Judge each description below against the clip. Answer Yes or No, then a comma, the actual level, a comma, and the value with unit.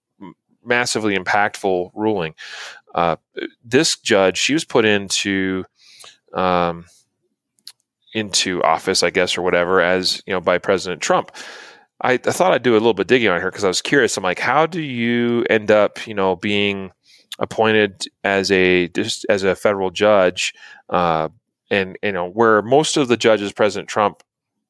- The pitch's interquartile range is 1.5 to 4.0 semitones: Yes, average, 3.5 semitones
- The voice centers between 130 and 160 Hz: No, low, 100 Hz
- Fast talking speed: No, average, 165 wpm